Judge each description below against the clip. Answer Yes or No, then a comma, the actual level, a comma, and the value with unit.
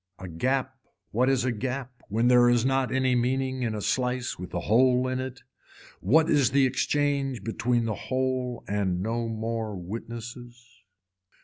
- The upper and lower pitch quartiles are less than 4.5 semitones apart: Yes, narrow, 2.5 semitones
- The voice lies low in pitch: Yes, low, 125 Hz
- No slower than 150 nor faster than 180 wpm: Yes, average, 165 wpm